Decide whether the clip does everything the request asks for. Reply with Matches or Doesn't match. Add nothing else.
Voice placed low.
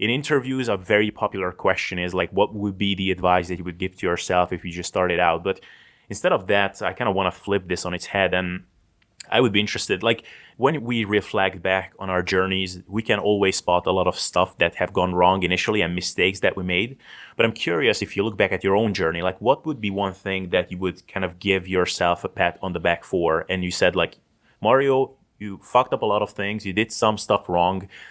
Matches